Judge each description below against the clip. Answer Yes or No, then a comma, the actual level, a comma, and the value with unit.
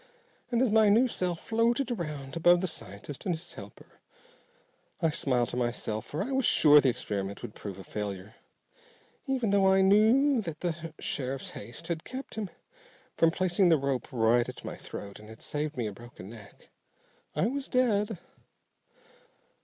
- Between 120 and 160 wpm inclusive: No, average, 175 wpm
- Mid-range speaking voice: Yes, medium, 165 Hz